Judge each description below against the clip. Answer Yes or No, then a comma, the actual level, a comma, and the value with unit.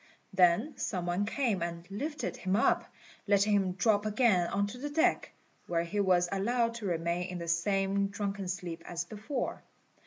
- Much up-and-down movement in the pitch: No, average, 3.4 semitones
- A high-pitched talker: Yes, high, 195 Hz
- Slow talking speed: No, average, 175 wpm